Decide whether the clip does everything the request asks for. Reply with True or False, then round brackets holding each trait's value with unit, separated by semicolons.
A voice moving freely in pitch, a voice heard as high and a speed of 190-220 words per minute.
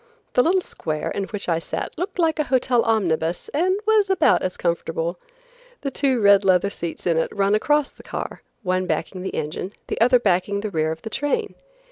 True (8.2 semitones; 200 Hz; 200 wpm)